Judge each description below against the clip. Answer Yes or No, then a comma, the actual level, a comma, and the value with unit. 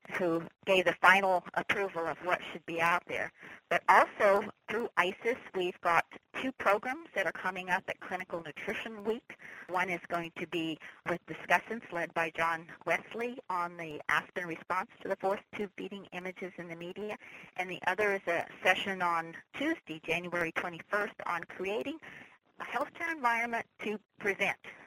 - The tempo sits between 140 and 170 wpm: Yes, average, 165 wpm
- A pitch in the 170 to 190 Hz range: Yes, medium, 185 Hz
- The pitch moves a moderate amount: Yes, average, 3.1 semitones